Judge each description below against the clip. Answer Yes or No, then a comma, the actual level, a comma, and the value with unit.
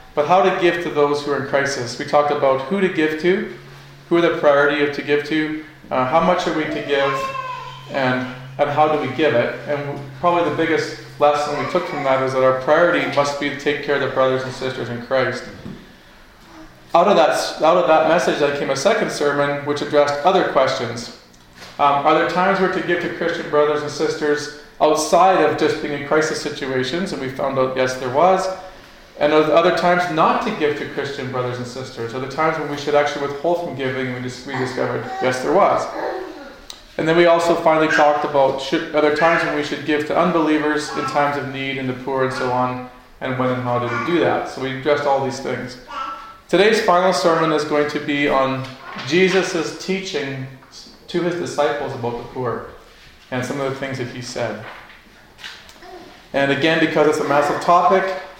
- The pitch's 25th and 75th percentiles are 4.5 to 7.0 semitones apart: No, average, 3.8 semitones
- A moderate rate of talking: No, fast, 210 wpm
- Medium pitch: Yes, medium, 145 Hz